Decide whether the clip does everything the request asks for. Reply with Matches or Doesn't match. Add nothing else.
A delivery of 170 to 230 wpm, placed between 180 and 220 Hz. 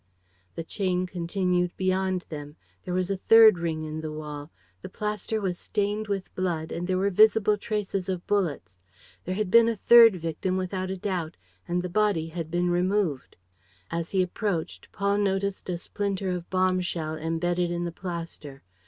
Matches